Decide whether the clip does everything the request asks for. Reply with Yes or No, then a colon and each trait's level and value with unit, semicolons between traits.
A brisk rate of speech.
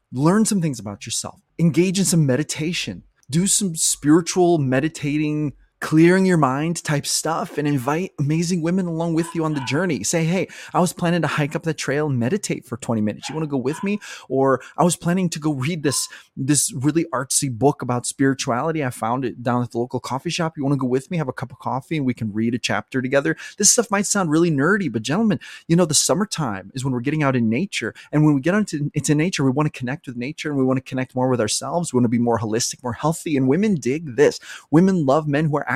Yes: fast, 245 wpm